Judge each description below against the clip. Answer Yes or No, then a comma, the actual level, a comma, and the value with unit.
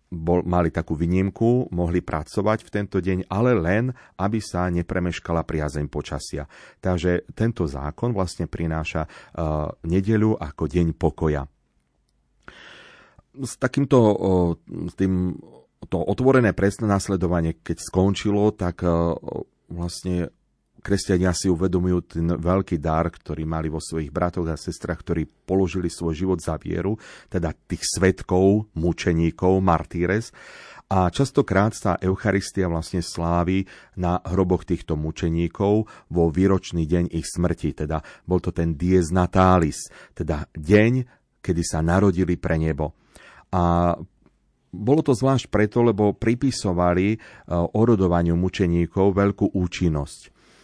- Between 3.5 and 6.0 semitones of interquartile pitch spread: No, average, 2.9 semitones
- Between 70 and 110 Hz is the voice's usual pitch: Yes, very low, 90 Hz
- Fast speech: No, average, 120 wpm